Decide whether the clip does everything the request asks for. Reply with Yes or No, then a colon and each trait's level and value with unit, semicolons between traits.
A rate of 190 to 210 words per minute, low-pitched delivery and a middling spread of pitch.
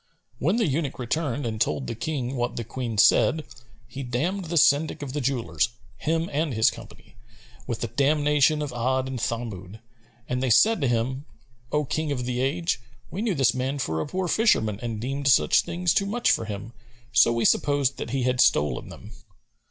Yes: average, 195 wpm; low, 130 Hz; average, 4.1 semitones